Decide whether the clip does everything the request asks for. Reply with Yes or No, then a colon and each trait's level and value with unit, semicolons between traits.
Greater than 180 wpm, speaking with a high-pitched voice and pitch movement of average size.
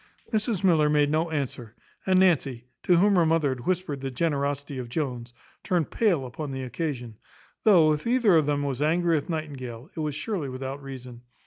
No: average, 190 wpm; medium, 150 Hz; average, 4.3 semitones